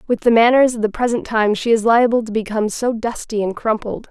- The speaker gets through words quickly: Yes, fast, 235 wpm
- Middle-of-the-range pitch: No, high, 225 Hz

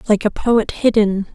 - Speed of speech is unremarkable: Yes, average, 180 wpm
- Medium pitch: No, high, 215 Hz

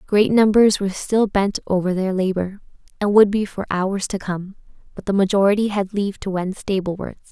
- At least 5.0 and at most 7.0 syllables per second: Yes, 5.4 syllables/s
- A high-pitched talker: Yes, high, 195 Hz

